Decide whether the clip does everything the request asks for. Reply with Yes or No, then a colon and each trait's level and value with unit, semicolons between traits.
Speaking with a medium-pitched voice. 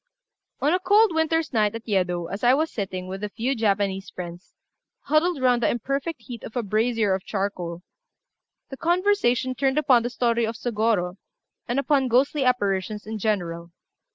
No: high, 230 Hz